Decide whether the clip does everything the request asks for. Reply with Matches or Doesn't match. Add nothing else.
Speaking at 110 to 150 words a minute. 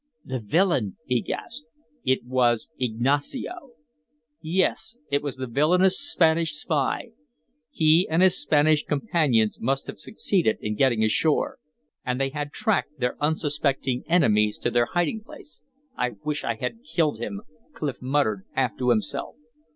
Matches